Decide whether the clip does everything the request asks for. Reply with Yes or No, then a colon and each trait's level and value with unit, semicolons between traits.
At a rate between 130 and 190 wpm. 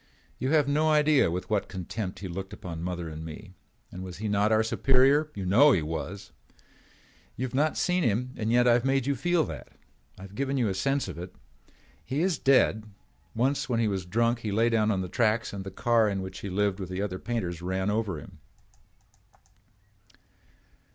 No: fast, 205 wpm